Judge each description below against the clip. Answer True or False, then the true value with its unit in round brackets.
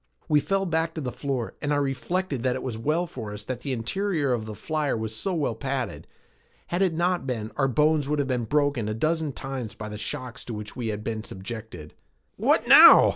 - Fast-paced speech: True (225 wpm)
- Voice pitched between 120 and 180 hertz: True (135 Hz)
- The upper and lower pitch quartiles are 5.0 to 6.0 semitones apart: True (5.6 semitones)